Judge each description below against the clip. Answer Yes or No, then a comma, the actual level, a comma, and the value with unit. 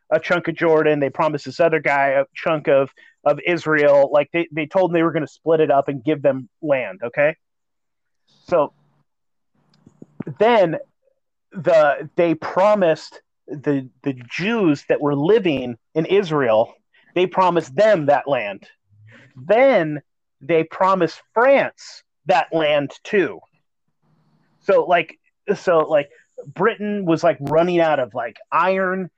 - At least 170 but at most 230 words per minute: No, average, 140 wpm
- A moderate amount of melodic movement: Yes, average, 3.6 semitones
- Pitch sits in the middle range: Yes, medium, 160 Hz